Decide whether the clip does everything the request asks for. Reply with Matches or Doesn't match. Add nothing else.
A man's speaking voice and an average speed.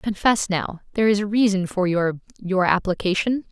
Doesn't match